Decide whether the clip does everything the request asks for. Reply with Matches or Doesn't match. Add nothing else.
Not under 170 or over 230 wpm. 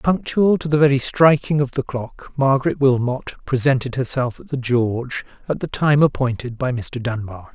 Matches